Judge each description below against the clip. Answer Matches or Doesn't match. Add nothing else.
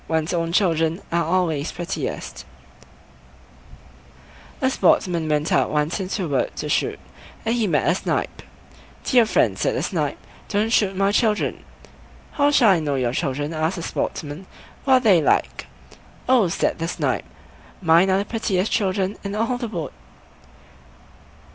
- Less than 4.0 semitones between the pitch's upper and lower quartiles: Doesn't match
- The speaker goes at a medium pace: Matches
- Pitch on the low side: Doesn't match